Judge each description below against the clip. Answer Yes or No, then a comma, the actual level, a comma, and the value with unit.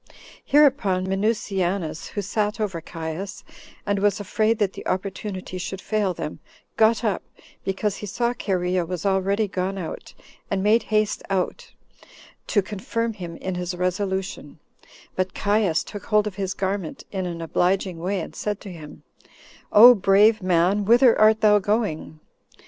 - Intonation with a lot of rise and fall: No, narrow, 2.5 semitones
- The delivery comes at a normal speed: Yes, average, 150 wpm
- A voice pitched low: No, high, 195 Hz